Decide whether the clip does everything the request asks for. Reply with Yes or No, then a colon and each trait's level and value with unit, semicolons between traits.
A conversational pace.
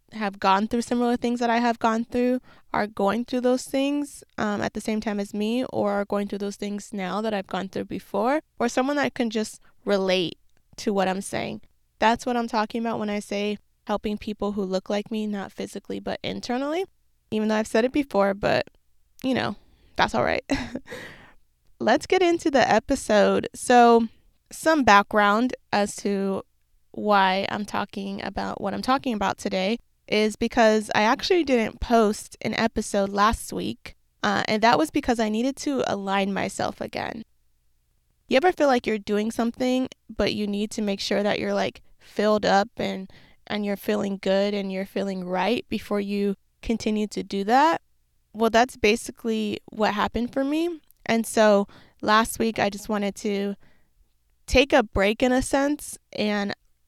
Yes: average, 180 wpm